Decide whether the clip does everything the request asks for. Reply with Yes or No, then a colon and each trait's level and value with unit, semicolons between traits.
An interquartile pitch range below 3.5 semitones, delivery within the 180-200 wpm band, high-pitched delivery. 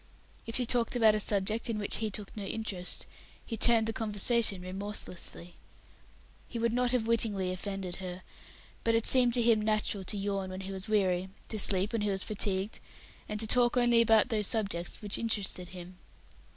Yes: average, 3.0 semitones; average, 190 wpm; high, 210 Hz